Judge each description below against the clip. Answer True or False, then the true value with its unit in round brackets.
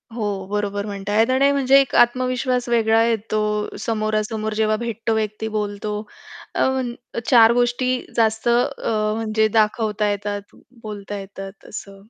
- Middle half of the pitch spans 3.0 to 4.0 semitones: False (2.4 semitones)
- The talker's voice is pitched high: True (220 Hz)